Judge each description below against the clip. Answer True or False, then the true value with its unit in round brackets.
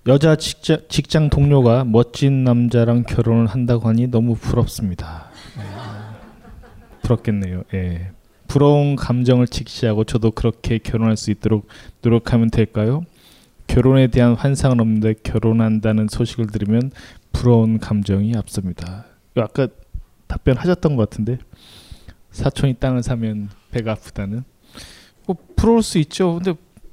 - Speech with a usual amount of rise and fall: True (3.3 semitones)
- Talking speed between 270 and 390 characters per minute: True (285 characters per minute)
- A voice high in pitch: False (115 Hz)